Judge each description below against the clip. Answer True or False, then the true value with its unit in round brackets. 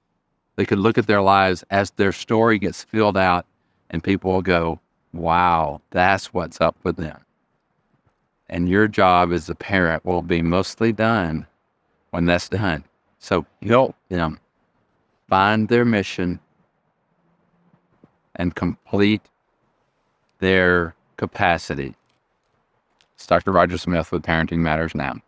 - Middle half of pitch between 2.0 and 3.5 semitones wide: True (2.8 semitones)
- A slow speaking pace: True (125 wpm)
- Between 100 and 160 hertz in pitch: False (90 Hz)